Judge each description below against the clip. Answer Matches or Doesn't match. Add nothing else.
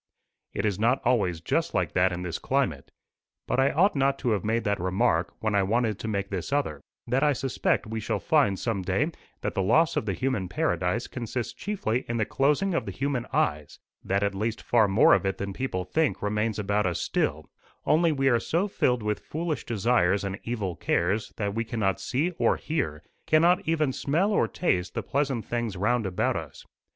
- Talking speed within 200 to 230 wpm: Matches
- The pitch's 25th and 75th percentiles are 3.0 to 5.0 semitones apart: Doesn't match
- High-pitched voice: Doesn't match